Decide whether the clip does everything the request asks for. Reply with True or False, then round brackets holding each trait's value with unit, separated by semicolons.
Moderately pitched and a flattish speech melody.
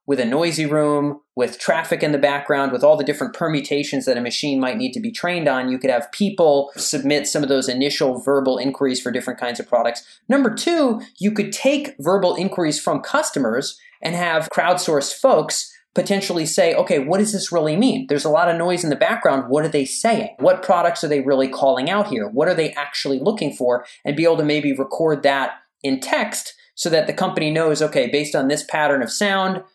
False (150 Hz; 4.7 semitones)